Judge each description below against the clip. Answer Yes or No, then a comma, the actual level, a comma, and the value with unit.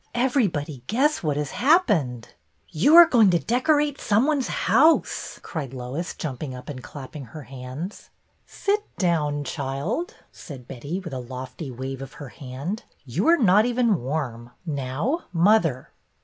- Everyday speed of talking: Yes, average, 150 wpm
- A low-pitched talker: No, medium, 155 Hz